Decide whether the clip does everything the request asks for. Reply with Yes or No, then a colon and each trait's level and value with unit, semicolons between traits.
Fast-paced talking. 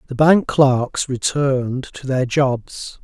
No: average, 140 wpm